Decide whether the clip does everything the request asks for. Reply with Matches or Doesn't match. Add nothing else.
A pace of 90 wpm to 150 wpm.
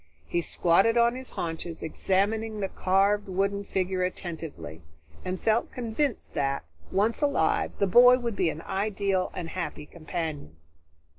Matches